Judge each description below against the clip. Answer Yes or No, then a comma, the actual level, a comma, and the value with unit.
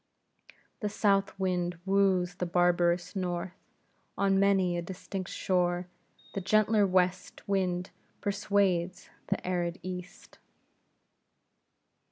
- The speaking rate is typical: No, slow, 100 wpm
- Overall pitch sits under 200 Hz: Yes, medium, 185 Hz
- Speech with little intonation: Yes, narrow, 1.8 semitones